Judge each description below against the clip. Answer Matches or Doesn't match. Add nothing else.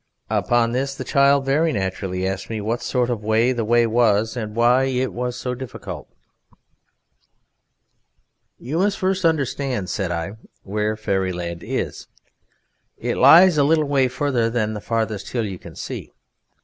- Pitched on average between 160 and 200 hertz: Doesn't match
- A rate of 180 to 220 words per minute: Doesn't match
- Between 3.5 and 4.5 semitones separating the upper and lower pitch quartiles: Matches